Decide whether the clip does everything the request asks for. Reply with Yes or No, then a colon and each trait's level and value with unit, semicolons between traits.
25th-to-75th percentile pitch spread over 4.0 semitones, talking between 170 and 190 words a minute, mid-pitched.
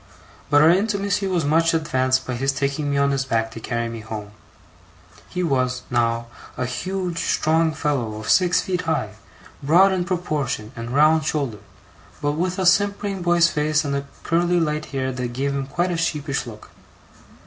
Yes: average, 5.2 semitones; average, 175 wpm; medium, 150 Hz